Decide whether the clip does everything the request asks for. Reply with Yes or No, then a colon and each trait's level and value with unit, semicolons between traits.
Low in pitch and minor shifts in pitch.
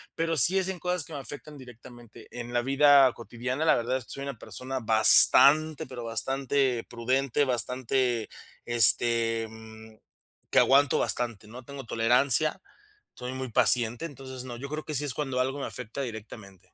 No: low, 130 Hz; average, 3.0 semitones